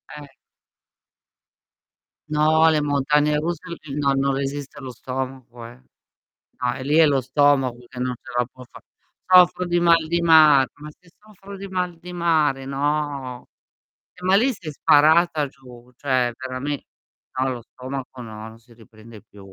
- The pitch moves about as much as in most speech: Yes, average, 3.9 semitones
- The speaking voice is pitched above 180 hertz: No, medium, 140 Hz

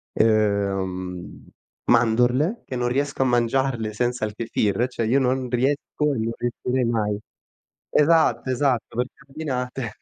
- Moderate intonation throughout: Yes, average, 3.1 semitones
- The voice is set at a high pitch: No, low, 120 Hz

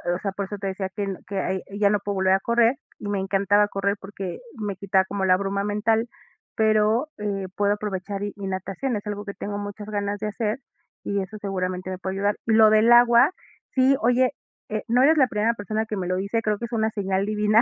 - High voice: Yes, high, 205 Hz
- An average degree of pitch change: No, narrow, 1.9 semitones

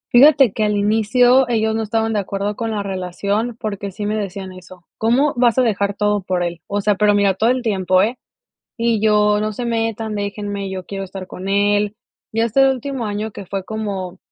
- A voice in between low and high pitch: No, high, 210 Hz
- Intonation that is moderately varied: No, narrow, 2.3 semitones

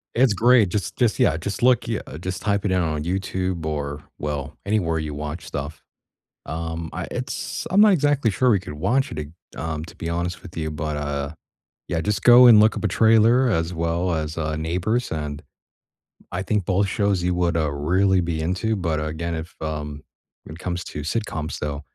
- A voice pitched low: Yes, very low, 85 Hz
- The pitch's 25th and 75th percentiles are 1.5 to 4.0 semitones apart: No, average, 5.0 semitones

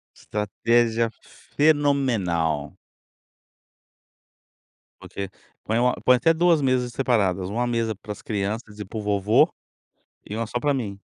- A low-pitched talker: Yes, low, 115 Hz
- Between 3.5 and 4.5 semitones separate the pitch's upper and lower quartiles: Yes, average, 3.8 semitones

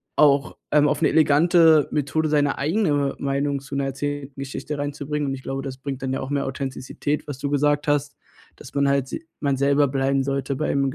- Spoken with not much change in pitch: Yes, narrow, 1.3 semitones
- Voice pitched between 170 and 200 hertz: No, medium, 140 Hz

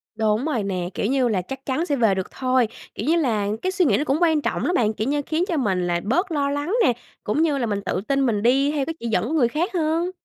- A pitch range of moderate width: No, wide, 6.3 semitones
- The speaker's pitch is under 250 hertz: No, very high, 270 Hz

